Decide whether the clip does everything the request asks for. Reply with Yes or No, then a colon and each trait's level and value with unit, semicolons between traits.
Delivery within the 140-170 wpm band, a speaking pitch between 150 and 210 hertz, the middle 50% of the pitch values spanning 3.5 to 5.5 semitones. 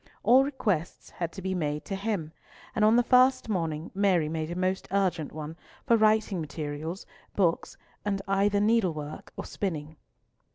Yes: average, 160 wpm; medium, 185 Hz; average, 4.8 semitones